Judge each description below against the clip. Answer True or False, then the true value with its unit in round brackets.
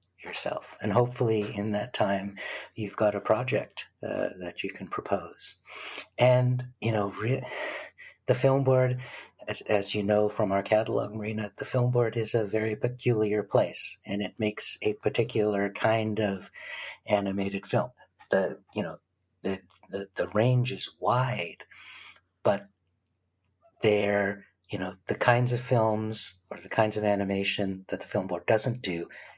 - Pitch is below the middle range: True (105 Hz)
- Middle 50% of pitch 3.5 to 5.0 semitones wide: False (3.1 semitones)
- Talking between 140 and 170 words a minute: True (155 wpm)